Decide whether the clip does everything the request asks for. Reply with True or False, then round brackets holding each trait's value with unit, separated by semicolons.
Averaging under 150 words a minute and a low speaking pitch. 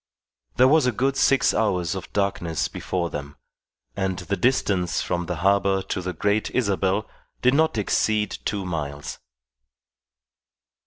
True (140 wpm; 100 Hz)